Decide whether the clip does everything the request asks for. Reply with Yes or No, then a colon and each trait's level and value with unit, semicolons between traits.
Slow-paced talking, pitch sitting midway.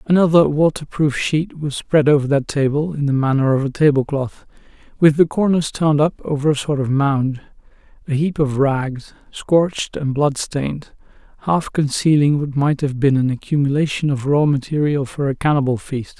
No: average, 170 wpm; medium, 145 Hz